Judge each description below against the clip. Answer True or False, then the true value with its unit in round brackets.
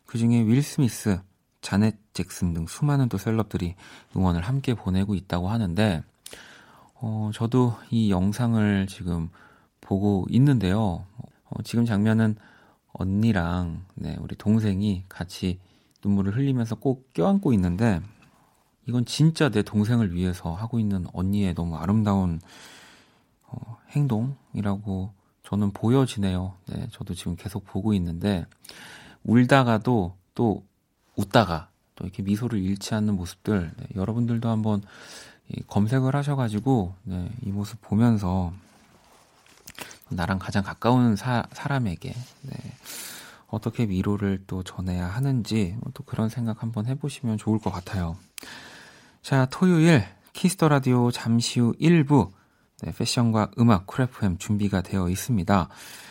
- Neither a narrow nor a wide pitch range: True (4.0 semitones)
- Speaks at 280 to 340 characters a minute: False (265 characters per minute)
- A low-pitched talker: True (105 Hz)